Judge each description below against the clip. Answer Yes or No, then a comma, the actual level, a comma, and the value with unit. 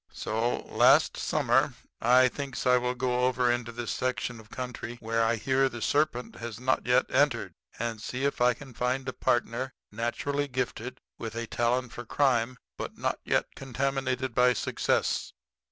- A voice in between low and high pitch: No, low, 125 Hz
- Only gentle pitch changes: Yes, narrow, 1.6 semitones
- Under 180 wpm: Yes, average, 170 wpm